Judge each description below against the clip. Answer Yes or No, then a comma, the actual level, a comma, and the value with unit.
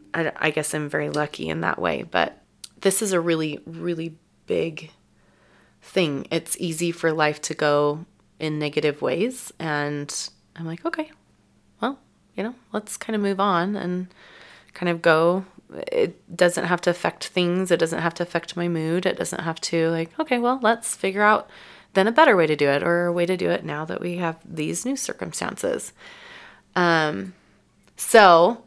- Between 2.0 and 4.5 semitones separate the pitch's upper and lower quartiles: Yes, average, 3.7 semitones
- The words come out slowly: No, average, 180 wpm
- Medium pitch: Yes, medium, 170 Hz